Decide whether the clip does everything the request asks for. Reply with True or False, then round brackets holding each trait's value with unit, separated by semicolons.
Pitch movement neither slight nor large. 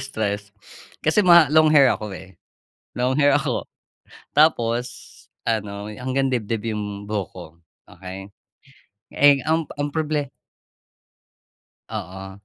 False (6.0 semitones)